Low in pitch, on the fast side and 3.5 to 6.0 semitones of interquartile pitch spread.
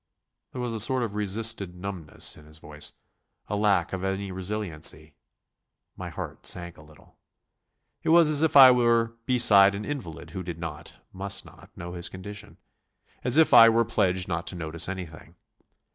No: low, 100 Hz; average, 175 wpm; average, 4.9 semitones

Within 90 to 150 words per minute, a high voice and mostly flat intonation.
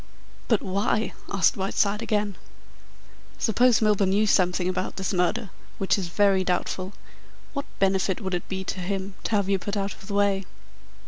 No: average, 170 wpm; high, 195 Hz; narrow, 1.5 semitones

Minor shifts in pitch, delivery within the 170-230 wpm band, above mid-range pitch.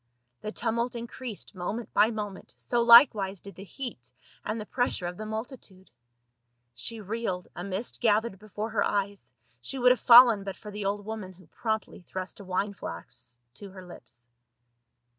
No: average, 3.4 semitones; average, 175 wpm; high, 205 Hz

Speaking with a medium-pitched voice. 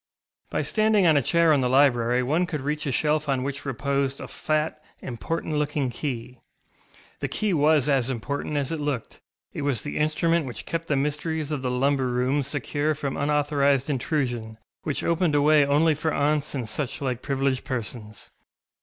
Yes: medium, 145 Hz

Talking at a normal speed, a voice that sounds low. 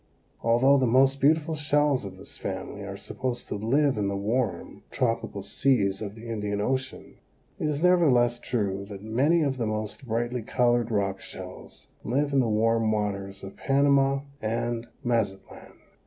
Yes: average, 160 wpm; low, 120 Hz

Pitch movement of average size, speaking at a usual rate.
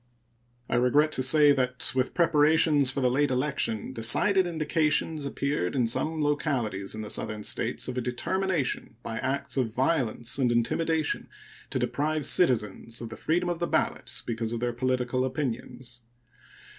Yes: average, 4.3 semitones; average, 155 wpm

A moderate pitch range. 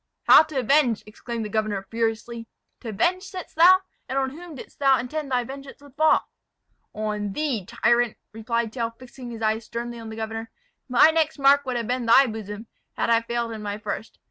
Yes: average, 3.6 semitones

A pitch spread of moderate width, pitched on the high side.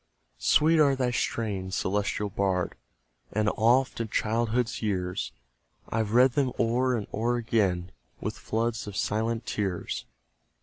No: average, 3.0 semitones; low, 110 Hz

